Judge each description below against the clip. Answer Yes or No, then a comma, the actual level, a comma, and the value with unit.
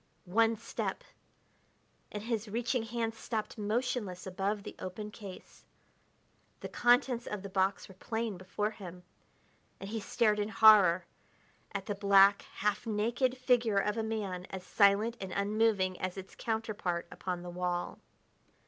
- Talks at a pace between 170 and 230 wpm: No, average, 145 wpm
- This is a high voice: Yes, high, 210 Hz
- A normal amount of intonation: Yes, average, 3.0 semitones